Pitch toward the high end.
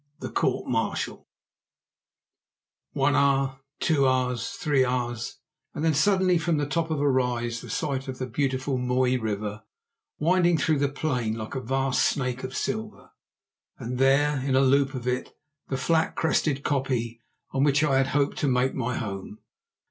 No: low, 135 Hz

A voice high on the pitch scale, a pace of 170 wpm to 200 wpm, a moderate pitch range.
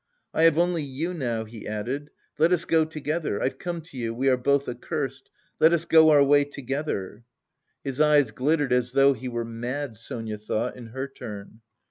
No: low, 135 Hz; average, 190 wpm; average, 4.4 semitones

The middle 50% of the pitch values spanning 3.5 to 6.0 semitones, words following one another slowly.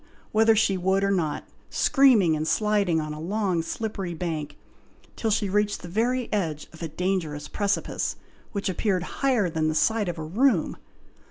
No: average, 4.7 semitones; average, 170 wpm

